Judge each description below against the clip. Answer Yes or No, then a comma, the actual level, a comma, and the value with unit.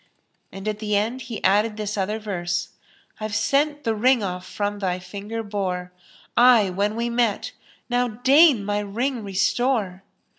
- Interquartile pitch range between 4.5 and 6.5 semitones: No, average, 3.2 semitones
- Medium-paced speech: Yes, average, 160 wpm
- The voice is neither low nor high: No, high, 215 Hz